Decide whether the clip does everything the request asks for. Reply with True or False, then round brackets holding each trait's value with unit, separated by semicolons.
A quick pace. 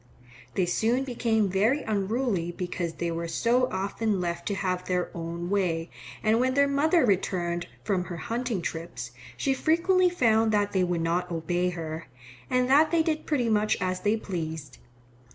False (170 wpm)